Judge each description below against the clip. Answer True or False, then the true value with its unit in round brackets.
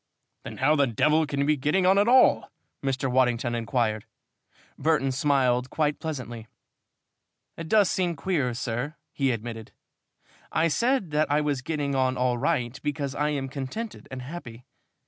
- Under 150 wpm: False (160 wpm)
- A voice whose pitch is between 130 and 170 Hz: True (140 Hz)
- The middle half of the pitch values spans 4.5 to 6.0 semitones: False (3.7 semitones)